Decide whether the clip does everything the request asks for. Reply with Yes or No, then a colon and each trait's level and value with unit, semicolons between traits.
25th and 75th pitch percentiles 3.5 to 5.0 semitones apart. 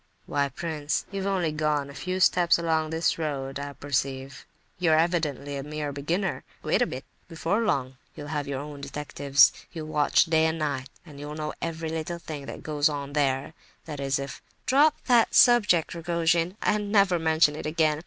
No: average, 2.9 semitones